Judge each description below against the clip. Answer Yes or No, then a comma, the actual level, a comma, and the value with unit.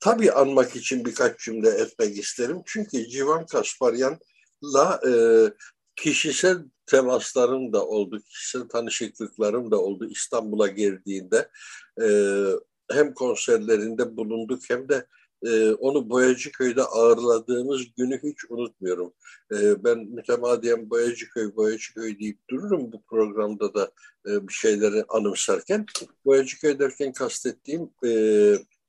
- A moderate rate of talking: Yes, average, 115 wpm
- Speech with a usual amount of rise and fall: No, wide, 8.2 semitones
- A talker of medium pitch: No, low, 130 Hz